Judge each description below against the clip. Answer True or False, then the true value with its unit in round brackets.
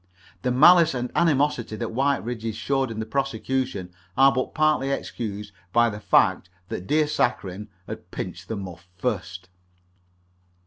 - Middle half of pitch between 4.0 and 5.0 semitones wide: True (4.6 semitones)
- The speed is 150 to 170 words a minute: False (140 wpm)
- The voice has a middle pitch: False (120 Hz)